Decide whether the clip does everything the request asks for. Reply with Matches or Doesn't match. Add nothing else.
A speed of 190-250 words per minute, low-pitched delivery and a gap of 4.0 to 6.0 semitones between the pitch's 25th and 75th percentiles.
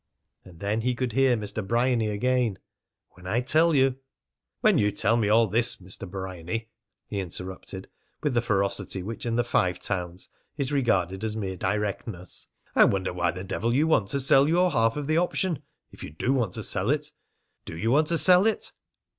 Matches